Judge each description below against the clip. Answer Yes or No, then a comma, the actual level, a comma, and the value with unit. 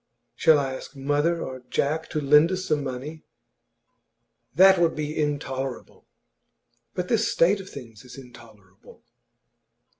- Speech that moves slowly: Yes, slow, 130 wpm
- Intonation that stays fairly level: No, average, 3.8 semitones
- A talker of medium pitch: Yes, medium, 145 Hz